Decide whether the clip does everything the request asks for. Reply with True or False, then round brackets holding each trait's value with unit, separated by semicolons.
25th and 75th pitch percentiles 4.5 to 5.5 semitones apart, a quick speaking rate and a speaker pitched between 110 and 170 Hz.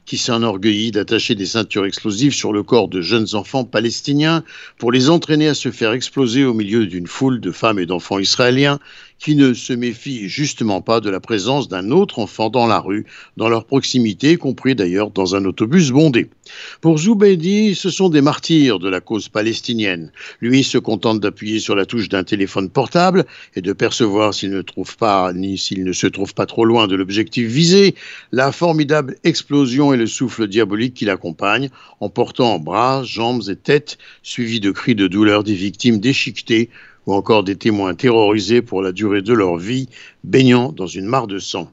True (4.8 semitones; 190 wpm; 115 Hz)